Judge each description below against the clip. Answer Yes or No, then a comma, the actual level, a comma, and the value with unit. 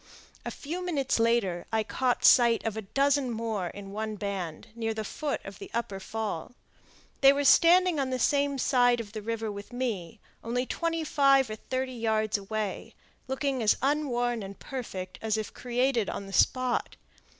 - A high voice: Yes, high, 235 Hz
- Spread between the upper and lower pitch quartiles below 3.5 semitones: No, average, 3.8 semitones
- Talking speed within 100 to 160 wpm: No, average, 175 wpm